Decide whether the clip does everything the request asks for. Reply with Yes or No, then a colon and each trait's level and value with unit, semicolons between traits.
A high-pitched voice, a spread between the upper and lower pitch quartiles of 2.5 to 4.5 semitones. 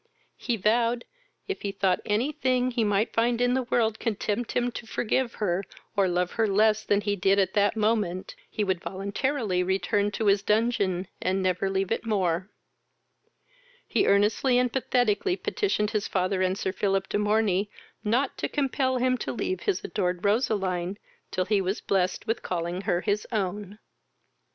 Yes: high, 205 Hz; average, 3.6 semitones